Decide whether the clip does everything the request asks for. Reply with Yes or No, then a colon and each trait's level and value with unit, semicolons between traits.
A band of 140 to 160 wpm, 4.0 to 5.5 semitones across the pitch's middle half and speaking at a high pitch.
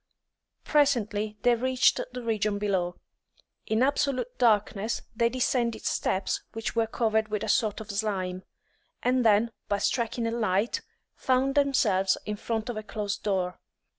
No: average, 145 wpm; average, 2.9 semitones; high, 220 Hz